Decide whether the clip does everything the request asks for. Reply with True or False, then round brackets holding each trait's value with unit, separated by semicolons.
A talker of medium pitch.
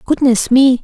False (255 Hz)